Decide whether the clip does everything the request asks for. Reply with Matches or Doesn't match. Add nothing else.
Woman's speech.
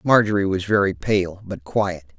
Doesn't match